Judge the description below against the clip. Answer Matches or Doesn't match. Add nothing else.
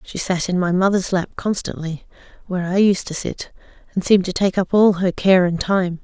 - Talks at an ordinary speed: Doesn't match